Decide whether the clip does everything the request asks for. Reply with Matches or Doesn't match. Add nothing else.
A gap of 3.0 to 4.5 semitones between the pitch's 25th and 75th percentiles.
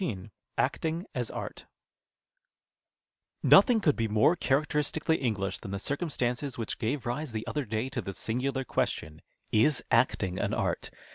Doesn't match